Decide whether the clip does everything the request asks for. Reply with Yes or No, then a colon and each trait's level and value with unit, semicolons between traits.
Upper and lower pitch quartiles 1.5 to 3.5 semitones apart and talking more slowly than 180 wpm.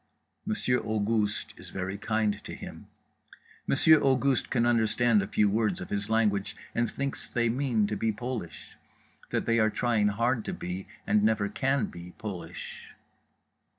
Yes: average, 2.8 semitones; average, 155 wpm